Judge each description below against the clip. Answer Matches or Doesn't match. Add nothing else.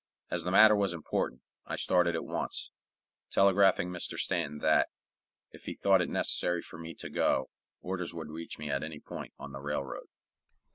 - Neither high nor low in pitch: Doesn't match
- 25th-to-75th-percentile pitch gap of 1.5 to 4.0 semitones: Matches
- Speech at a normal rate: Matches